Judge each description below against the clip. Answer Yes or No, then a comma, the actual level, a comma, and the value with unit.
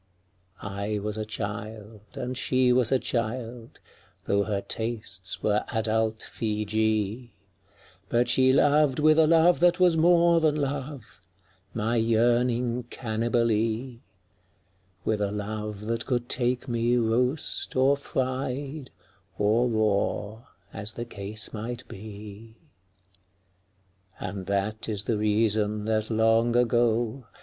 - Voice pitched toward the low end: Yes, low, 115 Hz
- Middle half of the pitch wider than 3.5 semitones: No, average, 2.9 semitones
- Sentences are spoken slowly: Yes, slow, 125 wpm